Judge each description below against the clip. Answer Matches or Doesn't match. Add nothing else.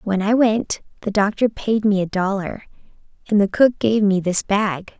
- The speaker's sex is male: Doesn't match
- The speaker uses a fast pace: Doesn't match